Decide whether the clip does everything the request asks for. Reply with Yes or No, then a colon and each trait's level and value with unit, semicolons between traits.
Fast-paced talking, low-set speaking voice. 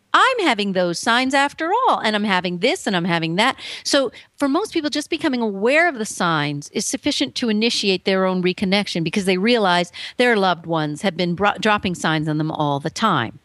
No: fast, 210 wpm; high, 205 Hz